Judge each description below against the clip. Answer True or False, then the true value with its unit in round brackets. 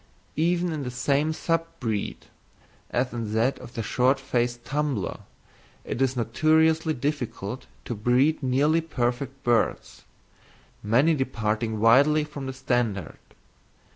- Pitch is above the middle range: False (130 Hz)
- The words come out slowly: True (125 wpm)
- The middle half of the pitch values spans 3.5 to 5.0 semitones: True (3.9 semitones)